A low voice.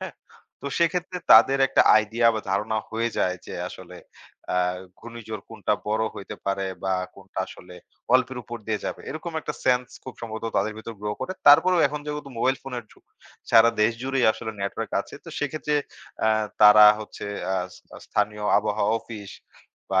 Yes: low, 115 Hz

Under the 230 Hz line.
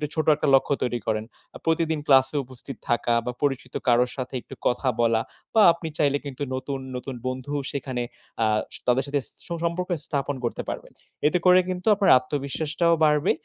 Yes: medium, 140 Hz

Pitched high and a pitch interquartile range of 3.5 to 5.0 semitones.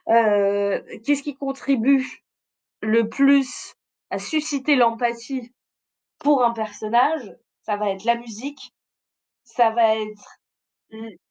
Yes: high, 235 Hz; average, 3.9 semitones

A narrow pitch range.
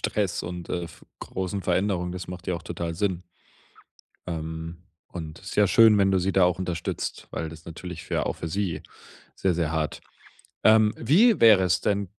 No: average, 3.1 semitones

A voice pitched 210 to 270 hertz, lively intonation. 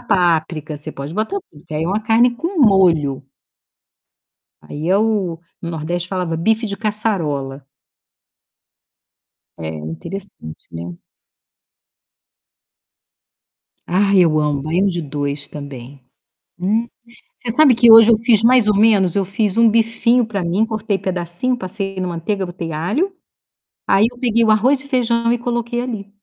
No: high, 195 Hz; wide, 5.7 semitones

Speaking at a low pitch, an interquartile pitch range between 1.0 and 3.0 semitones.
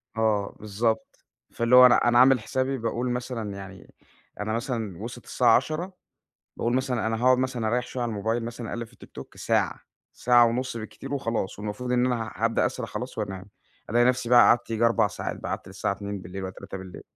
Yes: low, 115 Hz; narrow, 2.6 semitones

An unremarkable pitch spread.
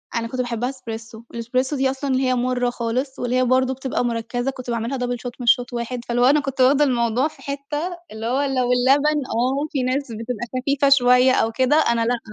No: narrow, 2.1 semitones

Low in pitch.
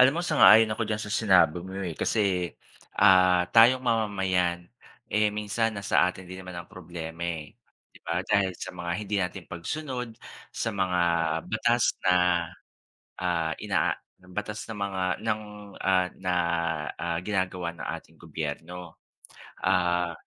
Yes: very low, 95 Hz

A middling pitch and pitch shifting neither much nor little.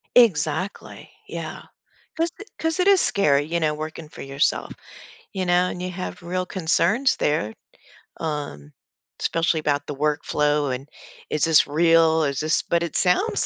Yes: medium, 160 Hz; average, 3.6 semitones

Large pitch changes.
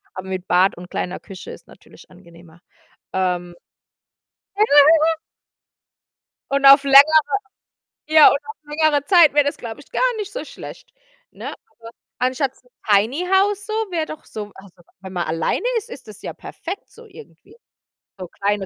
Yes: wide, 9.0 semitones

